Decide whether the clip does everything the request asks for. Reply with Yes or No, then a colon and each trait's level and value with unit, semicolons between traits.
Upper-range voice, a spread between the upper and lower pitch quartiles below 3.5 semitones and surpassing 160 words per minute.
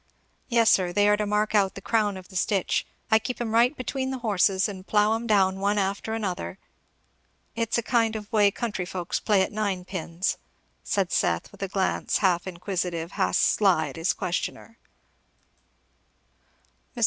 Yes: high, 205 Hz; average, 2.8 semitones; average, 170 wpm